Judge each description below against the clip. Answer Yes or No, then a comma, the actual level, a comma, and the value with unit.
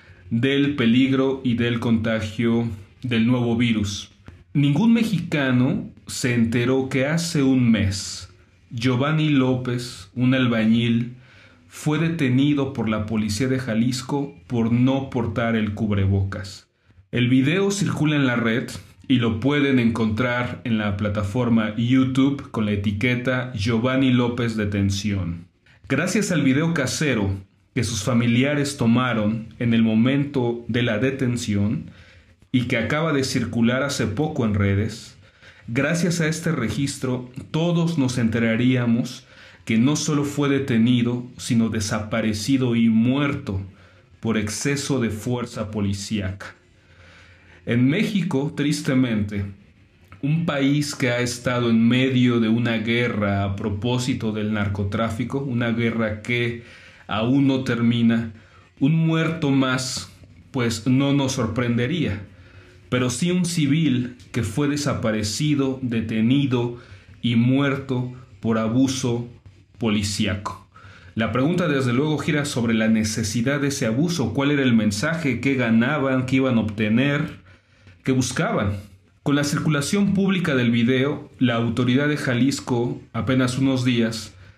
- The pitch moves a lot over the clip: No, average, 3.7 semitones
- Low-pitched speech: Yes, low, 120 Hz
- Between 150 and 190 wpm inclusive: No, slow, 125 wpm